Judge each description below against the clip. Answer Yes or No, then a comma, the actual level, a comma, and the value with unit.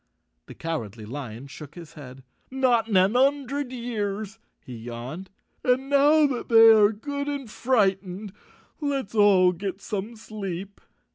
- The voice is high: Yes, high, 205 Hz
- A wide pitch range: Yes, wide, 6.0 semitones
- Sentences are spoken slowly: No, average, 150 wpm